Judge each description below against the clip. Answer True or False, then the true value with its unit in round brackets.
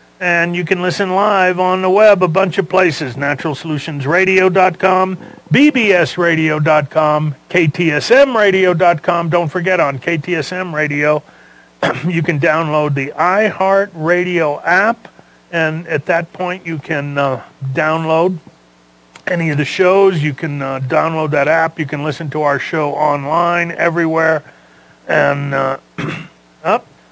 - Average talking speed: False (120 wpm)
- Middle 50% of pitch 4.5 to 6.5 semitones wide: False (3.5 semitones)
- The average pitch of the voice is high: False (160 Hz)